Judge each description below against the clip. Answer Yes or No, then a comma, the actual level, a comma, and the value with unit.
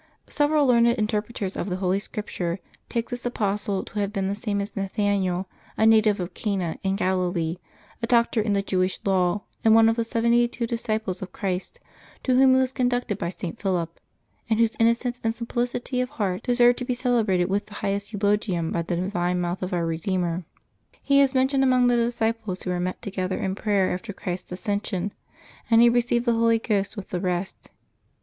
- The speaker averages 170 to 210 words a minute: Yes, average, 200 wpm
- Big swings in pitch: No, average, 4.1 semitones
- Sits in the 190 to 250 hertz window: Yes, high, 205 Hz